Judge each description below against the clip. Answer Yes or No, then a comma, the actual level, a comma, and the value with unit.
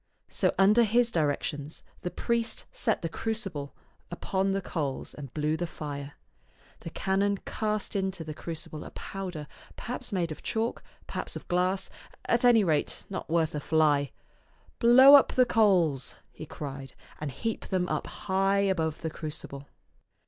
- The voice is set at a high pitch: No, medium, 180 Hz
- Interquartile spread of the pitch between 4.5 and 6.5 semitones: Yes, average, 5.0 semitones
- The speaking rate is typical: Yes, average, 160 wpm